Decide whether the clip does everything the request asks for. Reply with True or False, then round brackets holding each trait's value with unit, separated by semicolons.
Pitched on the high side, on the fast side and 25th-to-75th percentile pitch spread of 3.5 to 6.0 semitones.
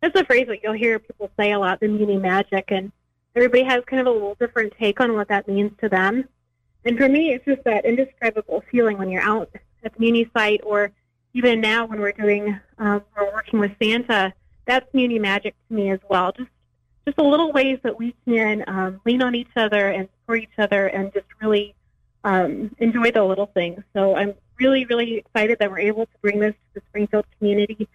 False (215 Hz; 215 wpm; 2.8 semitones)